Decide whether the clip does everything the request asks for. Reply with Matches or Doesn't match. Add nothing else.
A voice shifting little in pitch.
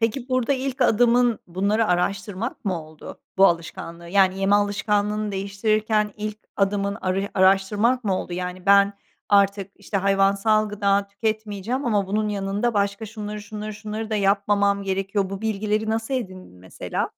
Matches